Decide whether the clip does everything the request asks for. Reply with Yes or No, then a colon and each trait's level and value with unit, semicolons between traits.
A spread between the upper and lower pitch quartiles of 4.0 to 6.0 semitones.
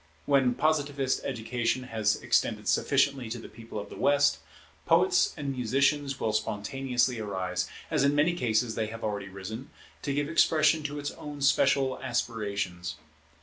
Yes: average, 4.6 semitones